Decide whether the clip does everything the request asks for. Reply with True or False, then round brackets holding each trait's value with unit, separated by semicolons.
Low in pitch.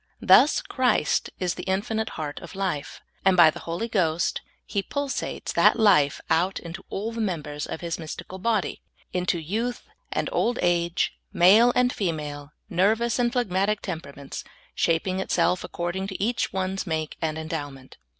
False (185 Hz)